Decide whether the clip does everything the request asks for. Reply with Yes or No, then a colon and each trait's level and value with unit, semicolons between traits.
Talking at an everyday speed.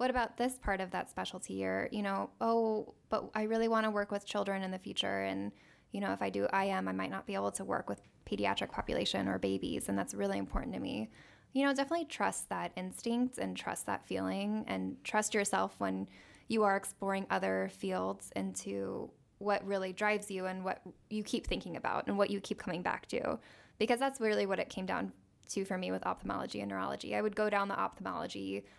No: fast, 220 wpm